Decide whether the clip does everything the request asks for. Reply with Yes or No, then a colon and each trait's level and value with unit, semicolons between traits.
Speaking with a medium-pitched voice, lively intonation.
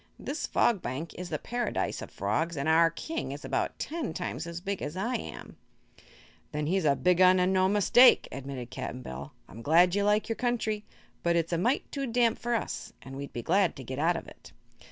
Yes: medium, 180 Hz; wide, 6.2 semitones